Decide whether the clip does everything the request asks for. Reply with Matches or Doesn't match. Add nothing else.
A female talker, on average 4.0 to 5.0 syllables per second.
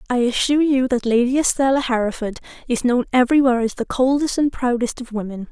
Doesn't match